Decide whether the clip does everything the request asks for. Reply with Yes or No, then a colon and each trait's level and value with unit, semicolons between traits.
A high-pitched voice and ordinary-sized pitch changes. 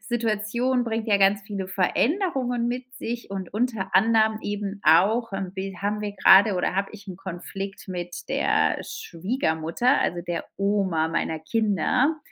Yes: high, 200 Hz; average, 3.5 semitones